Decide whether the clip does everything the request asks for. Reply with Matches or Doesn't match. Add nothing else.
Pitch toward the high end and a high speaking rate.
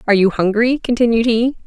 Doesn't match